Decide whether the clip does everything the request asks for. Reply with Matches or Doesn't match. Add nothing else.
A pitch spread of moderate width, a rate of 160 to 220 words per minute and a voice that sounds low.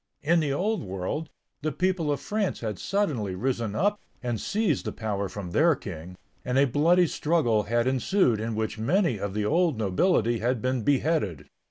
Doesn't match